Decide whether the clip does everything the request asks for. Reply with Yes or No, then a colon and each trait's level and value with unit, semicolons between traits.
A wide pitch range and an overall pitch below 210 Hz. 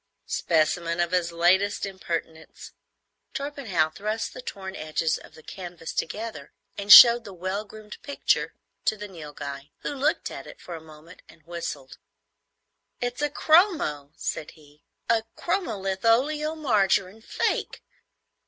Yes: wide, 5.8 semitones; high, 190 Hz